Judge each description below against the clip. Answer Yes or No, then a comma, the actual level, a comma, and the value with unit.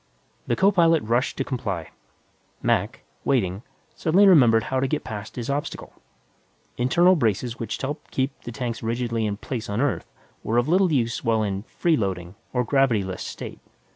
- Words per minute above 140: Yes, average, 170 wpm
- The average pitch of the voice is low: Yes, low, 120 Hz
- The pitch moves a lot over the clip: No, average, 4.6 semitones